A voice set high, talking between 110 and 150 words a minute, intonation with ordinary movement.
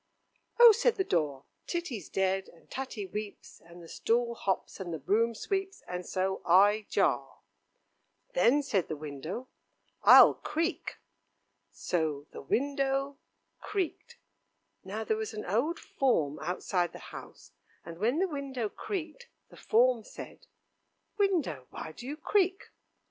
No: high, 220 Hz; average, 140 wpm; wide, 8.2 semitones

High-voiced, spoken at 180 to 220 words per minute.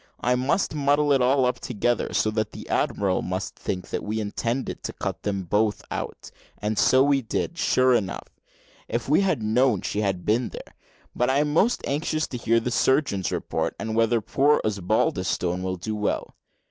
No: low, 115 Hz; average, 185 wpm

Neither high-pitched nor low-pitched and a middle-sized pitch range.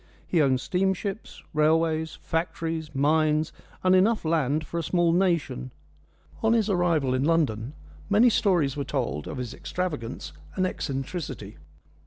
Yes: medium, 160 Hz; average, 4.7 semitones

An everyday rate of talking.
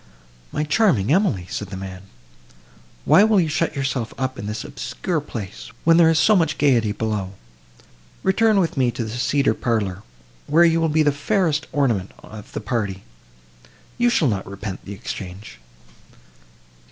Yes: average, 160 wpm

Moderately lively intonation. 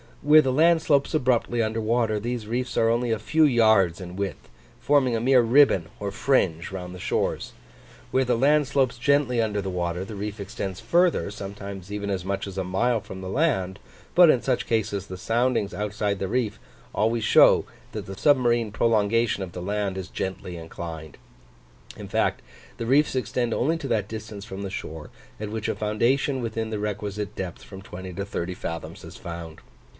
Yes: average, 4.2 semitones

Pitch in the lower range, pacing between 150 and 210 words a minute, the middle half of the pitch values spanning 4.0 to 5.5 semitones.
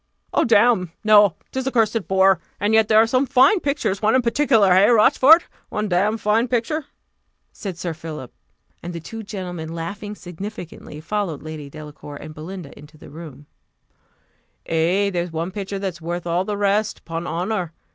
No: high, 195 Hz; average, 170 wpm; average, 4.7 semitones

